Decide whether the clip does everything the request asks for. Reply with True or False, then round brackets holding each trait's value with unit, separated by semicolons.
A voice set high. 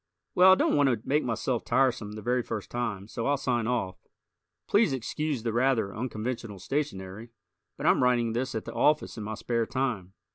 False (120 Hz)